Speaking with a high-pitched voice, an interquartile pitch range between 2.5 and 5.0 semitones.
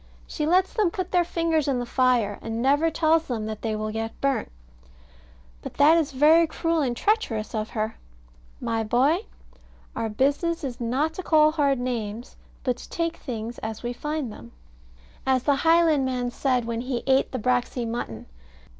No: very high, 260 Hz; wide, 5.4 semitones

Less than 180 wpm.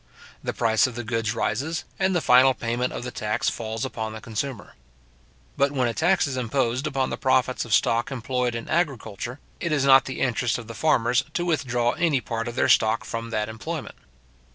No: average, 200 wpm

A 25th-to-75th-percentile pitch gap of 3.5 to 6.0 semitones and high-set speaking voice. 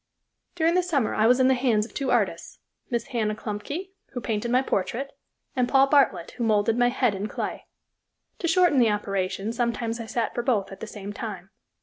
Yes: average, 3.9 semitones; high, 235 Hz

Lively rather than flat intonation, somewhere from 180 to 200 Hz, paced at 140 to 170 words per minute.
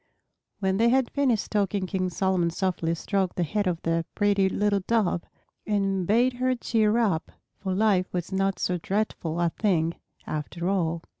No: average, 3.3 semitones; high, 190 Hz; average, 165 wpm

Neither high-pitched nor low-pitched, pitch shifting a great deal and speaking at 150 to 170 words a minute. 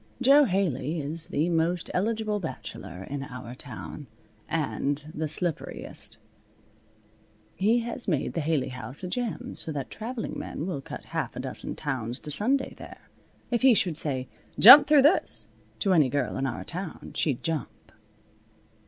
Yes: medium, 160 Hz; wide, 7.2 semitones; average, 155 wpm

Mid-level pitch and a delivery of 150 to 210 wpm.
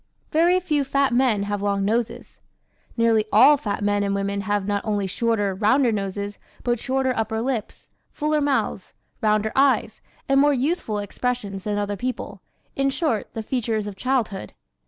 No: high, 225 Hz; average, 160 wpm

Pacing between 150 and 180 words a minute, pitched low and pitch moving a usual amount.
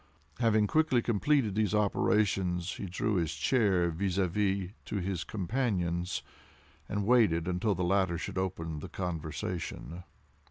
No: slow, 135 wpm; very low, 95 Hz; average, 3.3 semitones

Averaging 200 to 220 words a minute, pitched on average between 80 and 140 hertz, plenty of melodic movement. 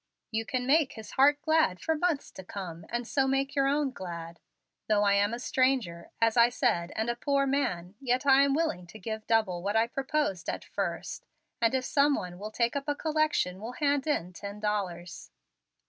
No: fast, 205 wpm; high, 235 Hz; wide, 5.8 semitones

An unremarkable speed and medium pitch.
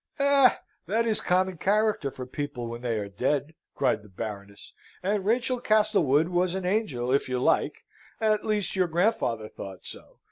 Yes: average, 175 wpm; medium, 175 Hz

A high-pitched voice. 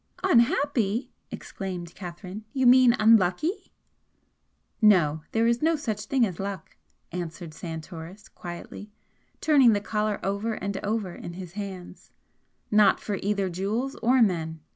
Yes: high, 200 Hz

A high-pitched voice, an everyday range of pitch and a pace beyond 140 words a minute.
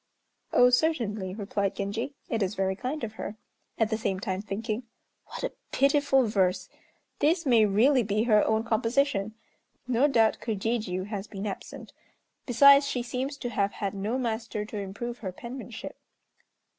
Yes: high, 220 Hz; average, 3.7 semitones; average, 155 wpm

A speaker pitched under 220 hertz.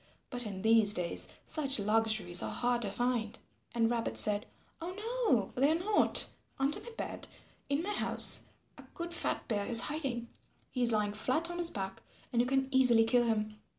No: high, 240 Hz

